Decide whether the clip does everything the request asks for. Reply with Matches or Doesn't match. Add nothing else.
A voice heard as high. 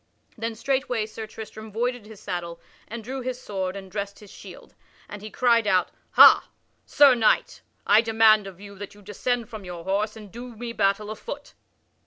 Matches